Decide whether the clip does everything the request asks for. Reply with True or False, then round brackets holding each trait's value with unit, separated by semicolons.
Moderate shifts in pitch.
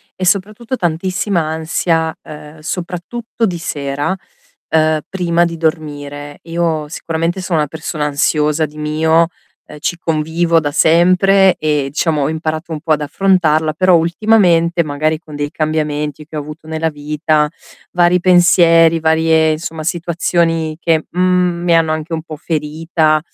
False (2.1 semitones)